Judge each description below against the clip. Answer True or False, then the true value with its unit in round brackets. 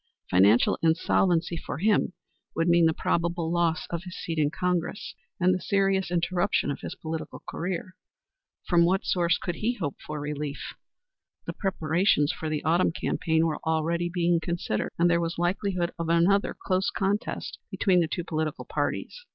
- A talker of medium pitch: True (170 Hz)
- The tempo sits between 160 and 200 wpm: True (165 wpm)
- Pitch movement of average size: False (2.2 semitones)